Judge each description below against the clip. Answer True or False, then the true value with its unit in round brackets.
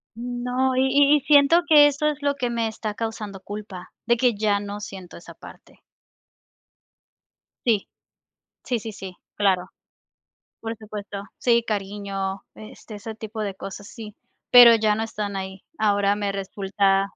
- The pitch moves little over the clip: False (3.2 semitones)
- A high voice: True (215 Hz)